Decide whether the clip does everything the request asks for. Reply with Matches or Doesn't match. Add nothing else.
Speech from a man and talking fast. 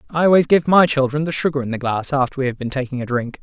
Matches